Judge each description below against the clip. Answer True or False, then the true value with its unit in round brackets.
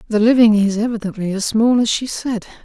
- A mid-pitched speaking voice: False (220 Hz)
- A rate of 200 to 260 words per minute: True (205 wpm)